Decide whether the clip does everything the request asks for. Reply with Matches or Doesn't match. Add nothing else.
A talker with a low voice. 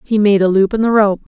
Doesn't match